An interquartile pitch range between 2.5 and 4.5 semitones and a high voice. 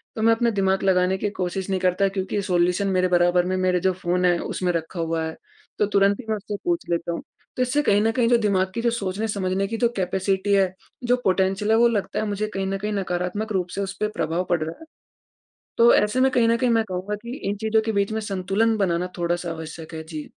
Yes: average, 3.2 semitones; high, 195 Hz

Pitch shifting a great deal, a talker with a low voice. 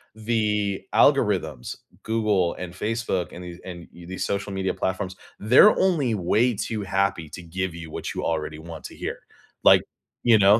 No: average, 3.8 semitones; very low, 95 Hz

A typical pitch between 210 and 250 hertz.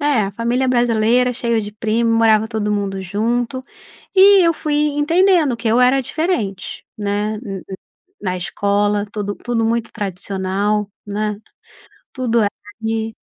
Yes: high, 225 Hz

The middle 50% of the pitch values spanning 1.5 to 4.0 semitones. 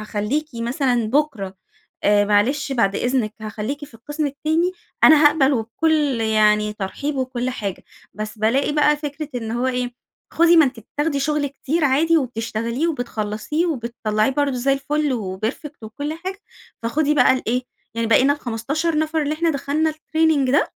No: average, 4.9 semitones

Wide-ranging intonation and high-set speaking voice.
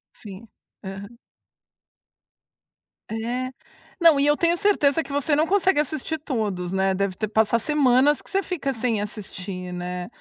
Yes: wide, 7.0 semitones; high, 245 Hz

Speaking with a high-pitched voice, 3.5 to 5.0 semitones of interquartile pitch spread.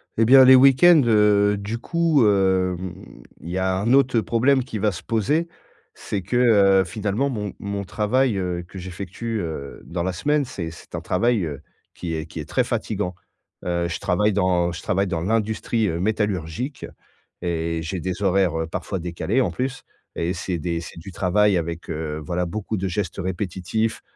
No: very low, 95 Hz; average, 4.4 semitones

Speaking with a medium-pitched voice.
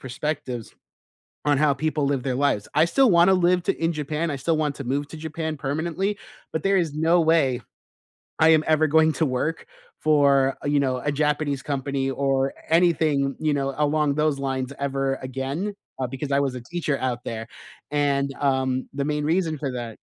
Yes: medium, 145 Hz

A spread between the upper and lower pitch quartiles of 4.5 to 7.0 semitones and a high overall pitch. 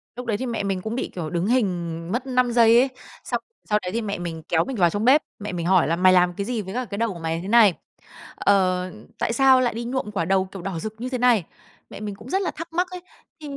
Yes: average, 5.2 semitones; high, 205 Hz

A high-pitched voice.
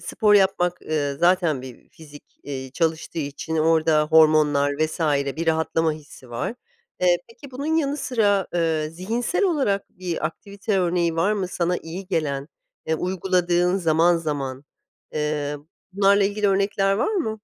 No: medium, 170 Hz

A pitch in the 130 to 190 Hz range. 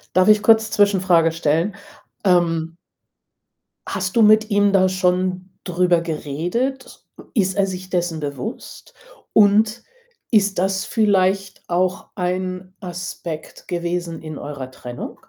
Yes: medium, 185 Hz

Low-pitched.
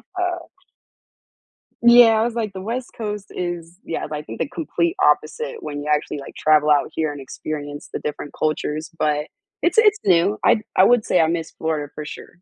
No: medium, 170 Hz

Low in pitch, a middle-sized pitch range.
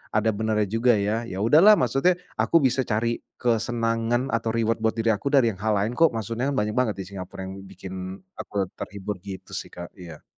Yes: low, 110 Hz; average, 3.2 semitones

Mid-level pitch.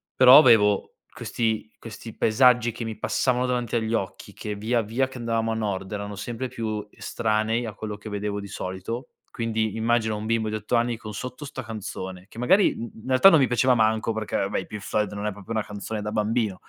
No: low, 110 Hz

